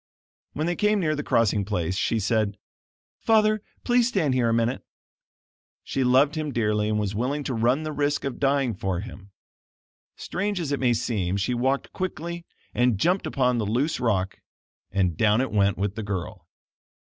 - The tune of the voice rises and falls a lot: Yes, wide, 6.1 semitones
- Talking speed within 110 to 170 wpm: No, average, 180 wpm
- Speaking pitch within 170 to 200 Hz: No, low, 125 Hz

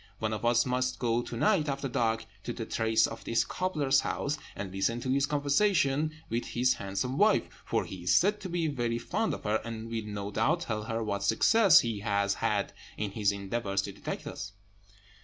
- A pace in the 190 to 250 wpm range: Yes, fast, 205 wpm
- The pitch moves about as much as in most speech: Yes, average, 4.9 semitones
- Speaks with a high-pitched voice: No, low, 120 Hz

